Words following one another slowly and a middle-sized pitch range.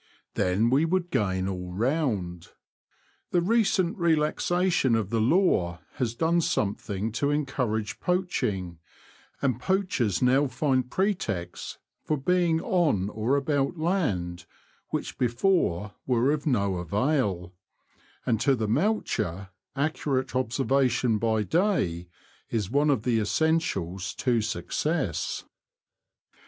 No: slow, 115 wpm; wide, 7.7 semitones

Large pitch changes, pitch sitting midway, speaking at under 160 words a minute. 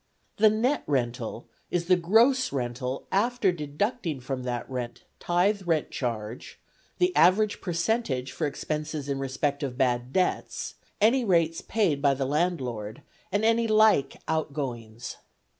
Yes: wide, 7.8 semitones; medium, 155 Hz; slow, 135 wpm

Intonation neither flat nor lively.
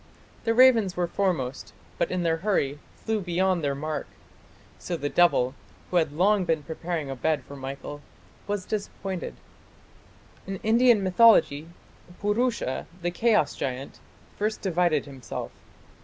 No: wide, 5.9 semitones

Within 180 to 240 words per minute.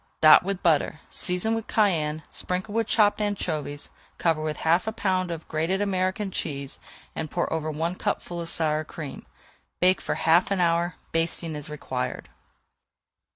No: average, 155 wpm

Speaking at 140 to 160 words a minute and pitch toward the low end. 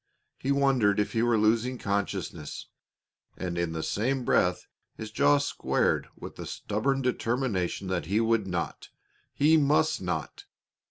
Yes: average, 145 wpm; low, 110 Hz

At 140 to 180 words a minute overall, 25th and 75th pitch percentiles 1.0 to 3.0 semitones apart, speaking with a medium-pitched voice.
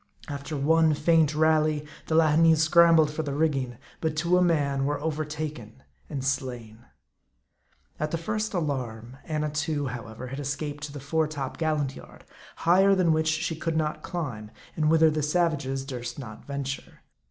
Yes: average, 160 wpm; average, 2.7 semitones; medium, 150 Hz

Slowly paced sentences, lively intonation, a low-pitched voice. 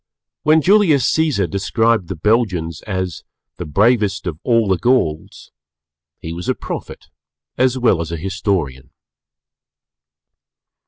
Yes: slow, 120 wpm; wide, 6.4 semitones; low, 100 Hz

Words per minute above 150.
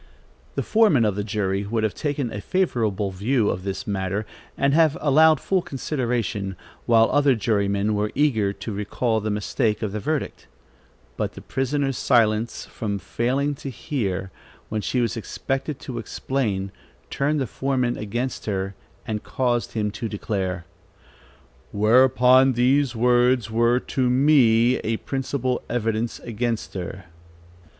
No: average, 140 wpm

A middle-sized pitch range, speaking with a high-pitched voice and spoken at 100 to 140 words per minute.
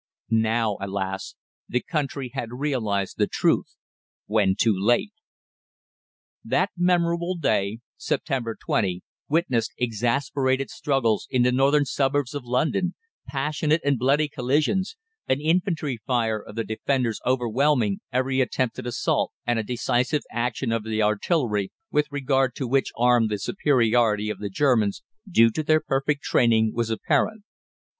No: average, 4.4 semitones; low, 125 Hz; slow, 135 wpm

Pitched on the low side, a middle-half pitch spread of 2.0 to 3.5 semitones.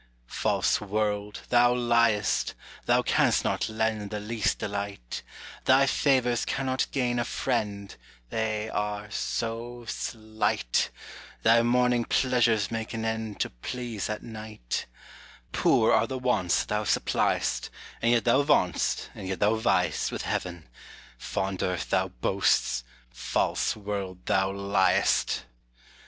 Yes: low, 110 Hz; average, 2.9 semitones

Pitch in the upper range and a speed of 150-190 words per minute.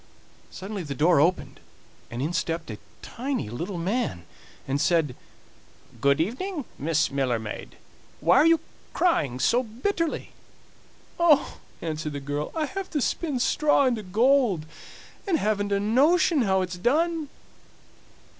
No: high, 200 Hz; slow, 135 wpm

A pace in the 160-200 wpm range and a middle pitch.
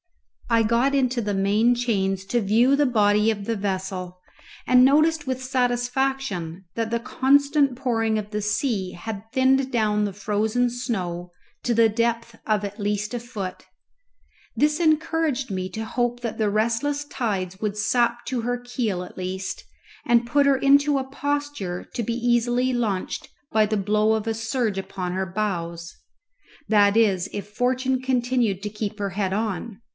No: average, 165 wpm; high, 225 Hz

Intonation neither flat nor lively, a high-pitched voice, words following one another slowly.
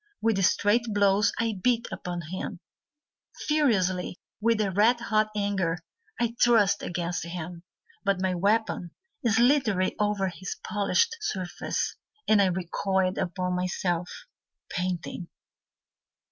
Yes: average, 3.6 semitones; high, 195 Hz; slow, 110 wpm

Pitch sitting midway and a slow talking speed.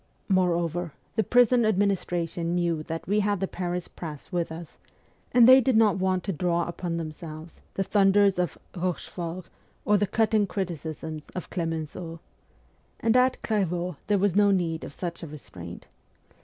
No: medium, 180 Hz; average, 155 wpm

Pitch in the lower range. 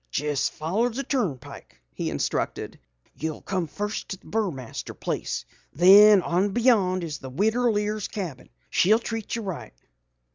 No: high, 195 Hz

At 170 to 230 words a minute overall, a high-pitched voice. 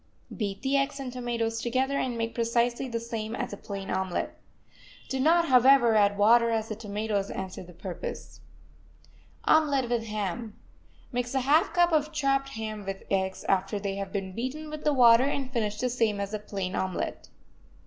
Yes: average, 185 wpm; high, 230 Hz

